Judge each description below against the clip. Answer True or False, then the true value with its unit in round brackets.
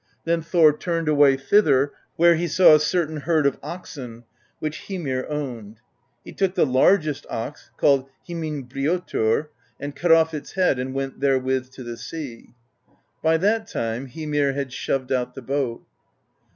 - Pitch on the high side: False (145 Hz)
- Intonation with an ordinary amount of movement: True (3.8 semitones)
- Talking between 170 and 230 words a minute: False (155 wpm)